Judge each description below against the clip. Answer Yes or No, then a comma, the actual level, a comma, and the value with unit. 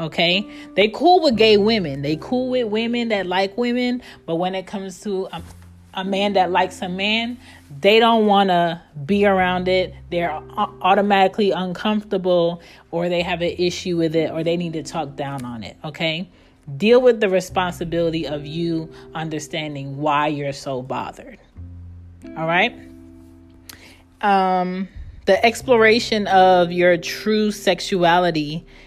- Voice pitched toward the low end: No, medium, 180 Hz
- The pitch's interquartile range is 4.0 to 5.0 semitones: Yes, average, 4.4 semitones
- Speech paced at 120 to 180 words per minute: Yes, average, 150 wpm